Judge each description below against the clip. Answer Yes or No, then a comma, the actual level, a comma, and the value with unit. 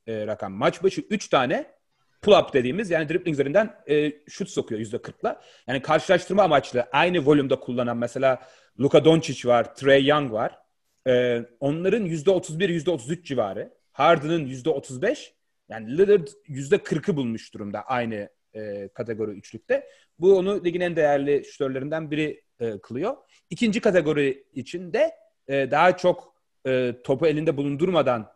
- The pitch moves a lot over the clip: Yes, wide, 6.0 semitones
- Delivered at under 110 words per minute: No, average, 135 wpm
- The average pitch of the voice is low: No, medium, 150 Hz